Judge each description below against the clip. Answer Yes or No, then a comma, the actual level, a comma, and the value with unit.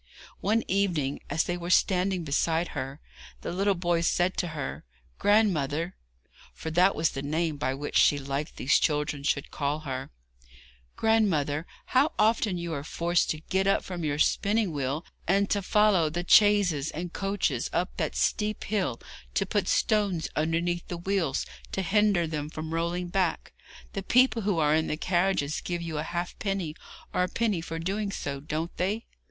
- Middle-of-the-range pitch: Yes, medium, 175 Hz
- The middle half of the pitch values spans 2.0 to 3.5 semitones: No, average, 4.2 semitones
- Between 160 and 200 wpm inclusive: Yes, average, 175 wpm